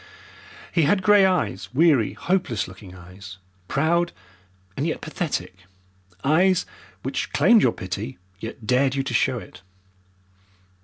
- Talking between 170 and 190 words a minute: No, slow, 135 wpm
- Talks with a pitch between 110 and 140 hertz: Yes, low, 135 Hz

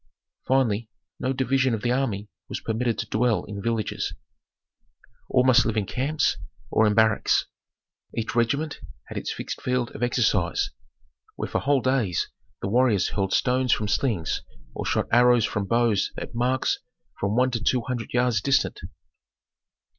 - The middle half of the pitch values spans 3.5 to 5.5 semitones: No, average, 3.0 semitones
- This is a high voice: No, low, 120 Hz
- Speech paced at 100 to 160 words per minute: Yes, average, 155 wpm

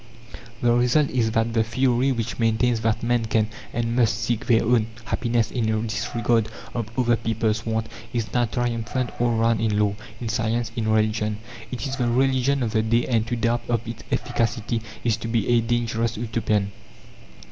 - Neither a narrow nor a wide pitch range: No, narrow, 1.4 semitones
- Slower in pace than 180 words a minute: No, average, 185 wpm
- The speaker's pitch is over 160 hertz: No, low, 115 Hz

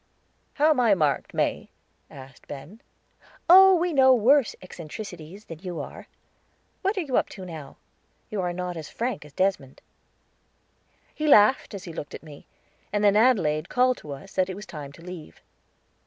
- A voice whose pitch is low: No, high, 190 Hz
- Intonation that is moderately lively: No, wide, 8.1 semitones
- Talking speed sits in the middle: Yes, average, 175 wpm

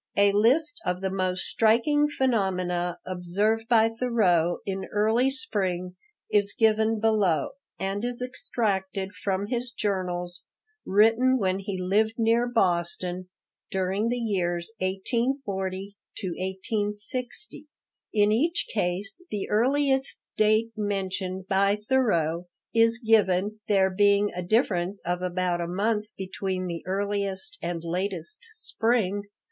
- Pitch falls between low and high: No, high, 200 Hz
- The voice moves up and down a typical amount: Yes, average, 3.5 semitones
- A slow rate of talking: Yes, slow, 120 wpm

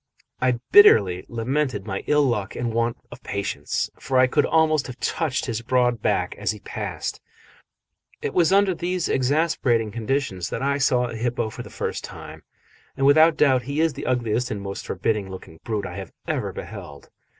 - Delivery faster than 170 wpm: Yes, average, 185 wpm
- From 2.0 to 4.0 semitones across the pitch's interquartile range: No, average, 4.8 semitones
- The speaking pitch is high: No, low, 125 Hz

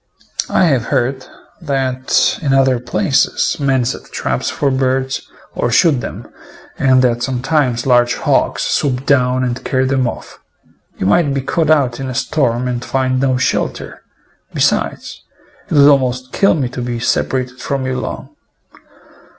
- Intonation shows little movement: Yes, narrow, 1.6 semitones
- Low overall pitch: Yes, low, 130 Hz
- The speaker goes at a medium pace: Yes, average, 155 wpm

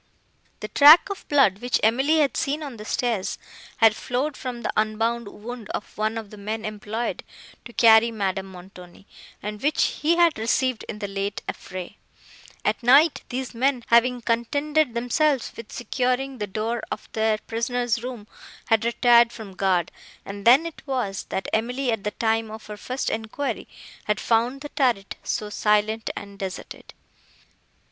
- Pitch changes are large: No, average, 3.3 semitones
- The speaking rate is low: No, average, 165 wpm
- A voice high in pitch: Yes, high, 230 Hz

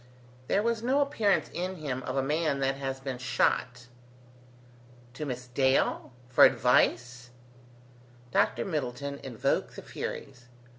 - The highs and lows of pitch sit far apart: No, average, 4.0 semitones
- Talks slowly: Yes, slow, 130 wpm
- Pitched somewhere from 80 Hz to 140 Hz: Yes, low, 135 Hz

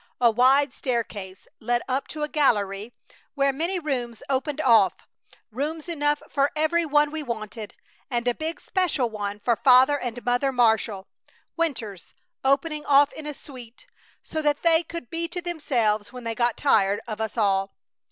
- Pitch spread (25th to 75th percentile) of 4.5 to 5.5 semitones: Yes, average, 4.9 semitones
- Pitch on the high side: Yes, very high, 260 Hz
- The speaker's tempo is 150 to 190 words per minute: Yes, average, 165 wpm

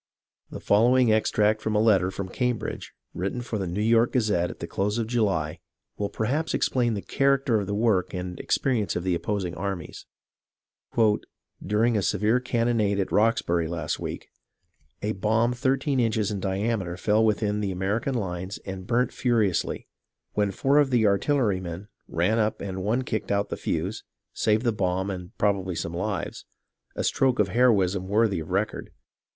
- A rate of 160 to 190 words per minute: Yes, average, 175 wpm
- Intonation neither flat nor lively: Yes, average, 3.5 semitones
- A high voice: No, low, 105 Hz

